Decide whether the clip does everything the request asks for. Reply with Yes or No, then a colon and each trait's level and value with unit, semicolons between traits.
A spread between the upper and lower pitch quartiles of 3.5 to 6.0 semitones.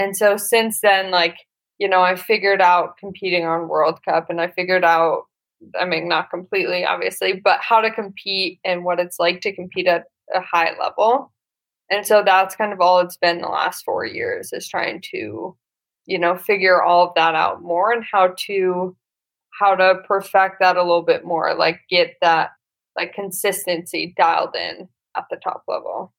No: average, 2.9 semitones